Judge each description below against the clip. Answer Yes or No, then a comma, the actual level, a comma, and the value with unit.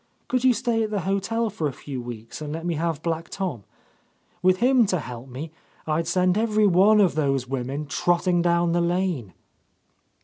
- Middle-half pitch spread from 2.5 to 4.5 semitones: No, average, 5.0 semitones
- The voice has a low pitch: No, medium, 170 Hz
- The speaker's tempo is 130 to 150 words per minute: No, average, 190 wpm